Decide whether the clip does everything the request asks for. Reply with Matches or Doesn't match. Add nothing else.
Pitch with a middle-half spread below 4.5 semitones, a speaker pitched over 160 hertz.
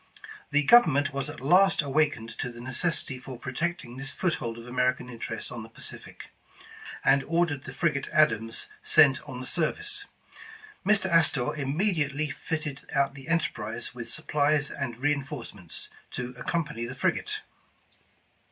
Doesn't match